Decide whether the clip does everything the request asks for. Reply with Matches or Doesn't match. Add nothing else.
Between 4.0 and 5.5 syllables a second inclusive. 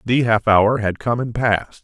Matches